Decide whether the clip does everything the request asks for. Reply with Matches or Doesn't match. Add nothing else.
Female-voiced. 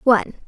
Matches